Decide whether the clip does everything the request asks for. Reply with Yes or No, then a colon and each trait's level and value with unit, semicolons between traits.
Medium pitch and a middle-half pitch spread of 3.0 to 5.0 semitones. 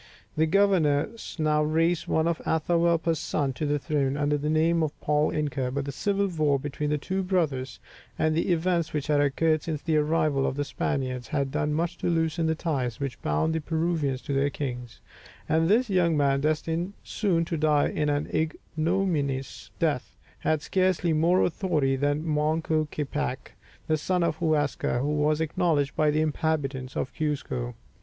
No: medium, 155 Hz; narrow, 2.4 semitones